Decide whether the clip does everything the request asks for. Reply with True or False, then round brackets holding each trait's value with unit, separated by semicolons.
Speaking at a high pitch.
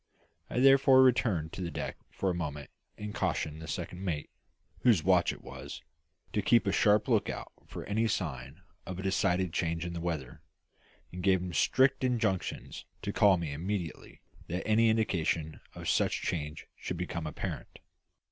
False (90 Hz)